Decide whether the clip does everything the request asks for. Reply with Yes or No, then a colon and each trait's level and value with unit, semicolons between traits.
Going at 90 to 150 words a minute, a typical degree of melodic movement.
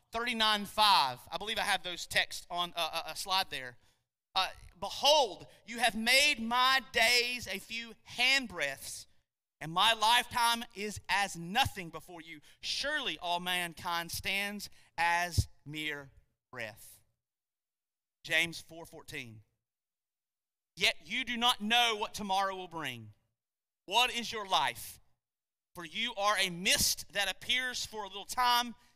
No: slow, 135 wpm; wide, 7.1 semitones